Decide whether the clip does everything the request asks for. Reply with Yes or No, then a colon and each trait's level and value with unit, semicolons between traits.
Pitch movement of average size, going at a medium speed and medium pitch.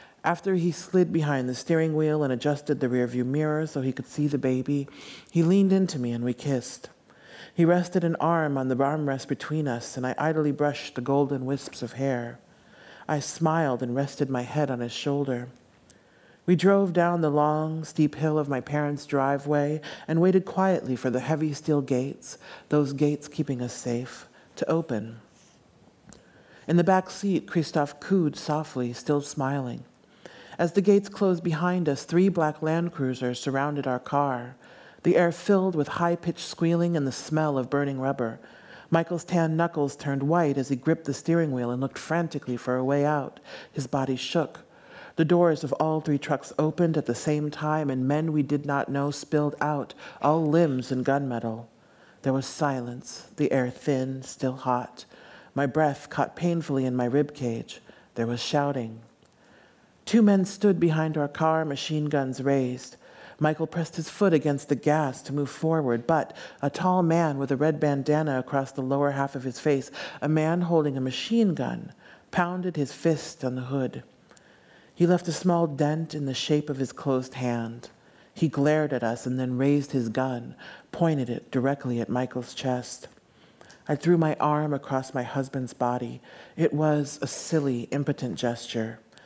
Yes: average, 3.4 semitones; average, 175 wpm; medium, 145 Hz